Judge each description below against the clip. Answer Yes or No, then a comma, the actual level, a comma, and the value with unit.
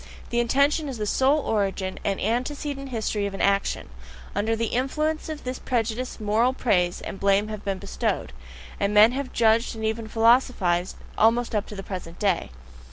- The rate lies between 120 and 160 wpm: No, average, 175 wpm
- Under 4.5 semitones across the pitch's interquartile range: Yes, average, 4.1 semitones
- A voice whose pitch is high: Yes, high, 225 Hz